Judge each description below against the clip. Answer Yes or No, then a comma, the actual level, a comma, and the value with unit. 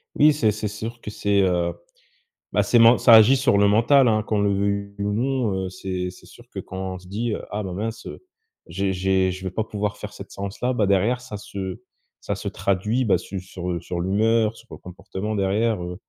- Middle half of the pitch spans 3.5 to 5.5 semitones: No, average, 3.0 semitones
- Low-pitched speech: Yes, low, 100 Hz